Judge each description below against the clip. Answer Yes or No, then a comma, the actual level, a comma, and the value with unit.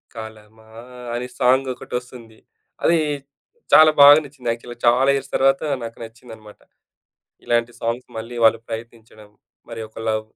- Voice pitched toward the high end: No, low, 115 Hz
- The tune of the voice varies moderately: No, narrow, 2.0 semitones